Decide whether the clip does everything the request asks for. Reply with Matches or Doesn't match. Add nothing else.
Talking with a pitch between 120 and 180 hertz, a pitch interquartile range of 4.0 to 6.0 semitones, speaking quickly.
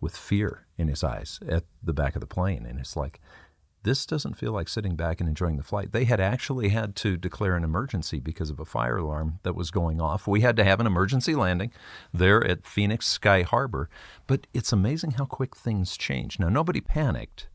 Doesn't match